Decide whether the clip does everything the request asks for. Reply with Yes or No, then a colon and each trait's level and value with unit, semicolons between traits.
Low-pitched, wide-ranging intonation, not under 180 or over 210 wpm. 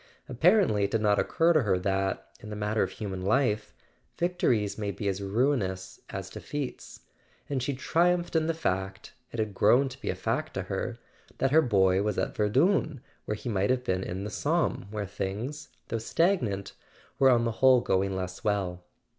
Yes: low, 110 Hz; wide, 5.7 semitones; average, 185 wpm